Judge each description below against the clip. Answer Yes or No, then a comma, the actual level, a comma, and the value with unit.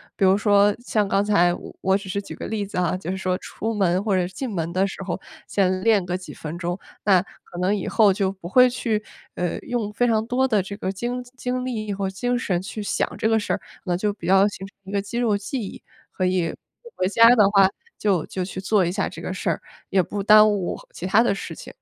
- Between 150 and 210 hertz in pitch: Yes, high, 200 Hz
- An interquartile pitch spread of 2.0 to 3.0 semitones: Yes, narrow, 2.5 semitones